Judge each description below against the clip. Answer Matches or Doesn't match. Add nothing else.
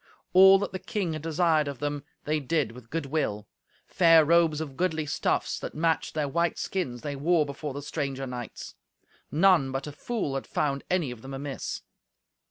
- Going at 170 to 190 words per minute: Matches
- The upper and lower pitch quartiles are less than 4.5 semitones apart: Matches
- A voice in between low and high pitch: Matches